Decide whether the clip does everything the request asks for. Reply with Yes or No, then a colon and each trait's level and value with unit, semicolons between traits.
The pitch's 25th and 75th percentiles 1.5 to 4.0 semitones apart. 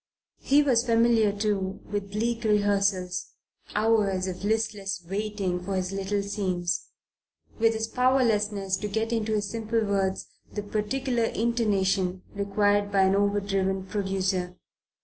Yes: narrow, 2.4 semitones